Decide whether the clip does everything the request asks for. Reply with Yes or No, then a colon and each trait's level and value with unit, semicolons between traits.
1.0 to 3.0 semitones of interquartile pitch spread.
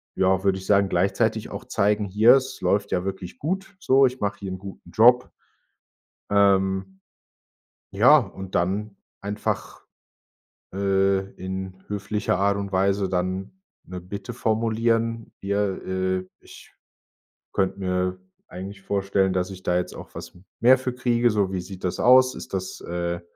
Yes: narrow, 2.6 semitones